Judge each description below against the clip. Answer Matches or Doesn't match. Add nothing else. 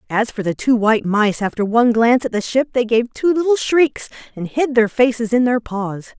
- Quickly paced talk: Matches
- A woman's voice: Matches